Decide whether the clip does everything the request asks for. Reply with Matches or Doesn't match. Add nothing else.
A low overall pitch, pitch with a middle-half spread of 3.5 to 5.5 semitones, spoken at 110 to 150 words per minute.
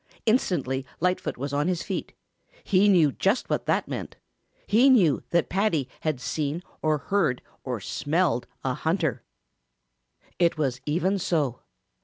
Doesn't match